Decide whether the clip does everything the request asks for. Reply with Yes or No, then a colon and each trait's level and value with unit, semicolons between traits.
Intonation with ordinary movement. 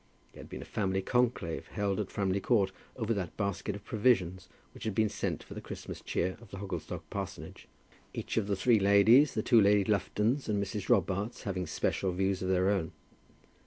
No: narrow, 2.3 semitones